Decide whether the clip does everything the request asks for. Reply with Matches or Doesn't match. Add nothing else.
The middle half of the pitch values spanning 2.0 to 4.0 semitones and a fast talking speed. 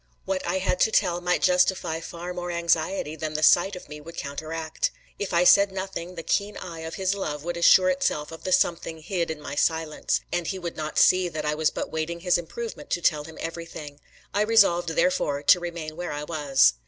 Matches